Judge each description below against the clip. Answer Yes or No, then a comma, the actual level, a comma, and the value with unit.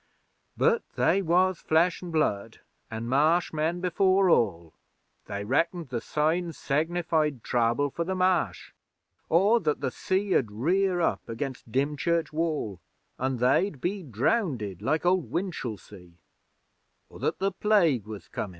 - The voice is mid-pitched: Yes, medium, 155 Hz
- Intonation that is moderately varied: No, wide, 6.9 semitones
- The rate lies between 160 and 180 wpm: No, average, 140 wpm